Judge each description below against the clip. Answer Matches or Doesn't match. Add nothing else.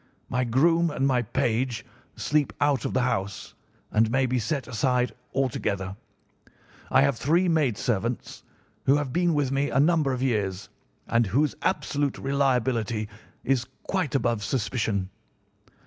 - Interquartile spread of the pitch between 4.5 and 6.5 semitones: Doesn't match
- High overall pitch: Doesn't match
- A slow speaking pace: Doesn't match